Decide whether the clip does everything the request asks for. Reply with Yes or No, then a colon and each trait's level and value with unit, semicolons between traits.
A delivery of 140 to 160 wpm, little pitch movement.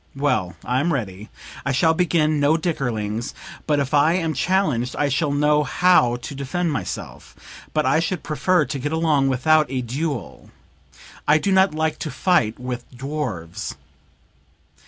No: average, 155 wpm; average, 4.2 semitones